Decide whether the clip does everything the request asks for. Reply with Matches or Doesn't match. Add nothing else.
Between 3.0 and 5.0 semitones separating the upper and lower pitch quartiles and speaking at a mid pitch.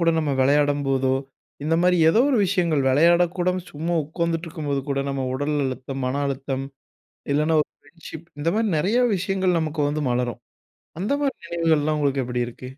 Matches